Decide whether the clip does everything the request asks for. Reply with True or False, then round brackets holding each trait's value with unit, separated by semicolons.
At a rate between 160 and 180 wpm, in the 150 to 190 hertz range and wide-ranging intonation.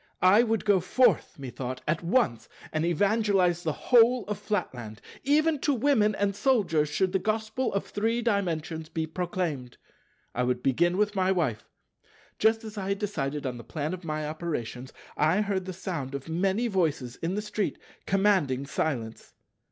True (165 wpm; 185 Hz; 5.8 semitones)